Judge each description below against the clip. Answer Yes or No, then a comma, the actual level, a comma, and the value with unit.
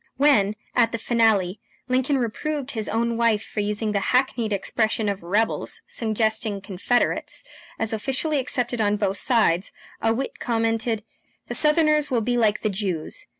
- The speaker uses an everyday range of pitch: Yes, average, 3.1 semitones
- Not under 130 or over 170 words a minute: Yes, average, 150 wpm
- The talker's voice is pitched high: Yes, high, 225 Hz